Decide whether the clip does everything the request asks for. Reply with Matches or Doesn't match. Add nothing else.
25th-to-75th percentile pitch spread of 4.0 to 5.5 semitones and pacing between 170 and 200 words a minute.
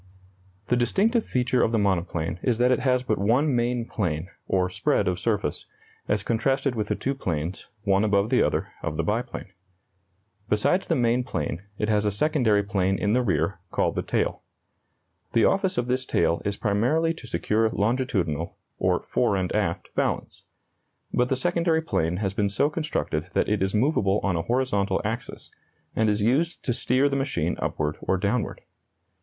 Matches